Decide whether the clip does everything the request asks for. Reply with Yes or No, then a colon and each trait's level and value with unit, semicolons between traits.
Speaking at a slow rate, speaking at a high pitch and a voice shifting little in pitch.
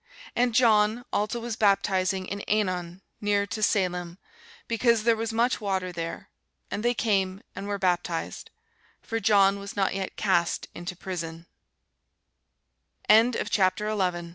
No: slow, 125 wpm; high, 200 Hz; average, 3.0 semitones